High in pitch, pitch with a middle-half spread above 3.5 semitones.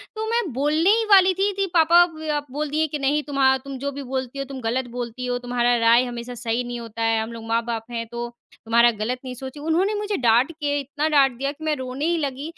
Yes: very high, 270 Hz; average, 4.1 semitones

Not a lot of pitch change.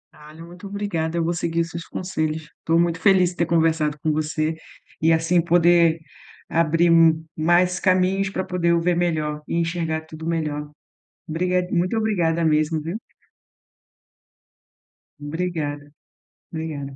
Yes: narrow, 1.8 semitones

